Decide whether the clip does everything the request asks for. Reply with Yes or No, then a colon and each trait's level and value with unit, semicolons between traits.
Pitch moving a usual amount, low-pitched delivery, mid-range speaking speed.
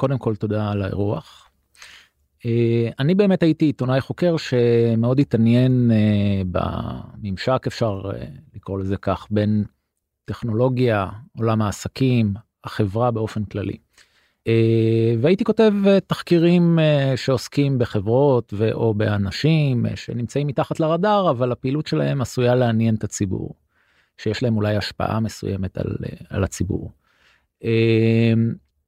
Yes: average, 4.0 semitones; low, 115 Hz; average, 120 wpm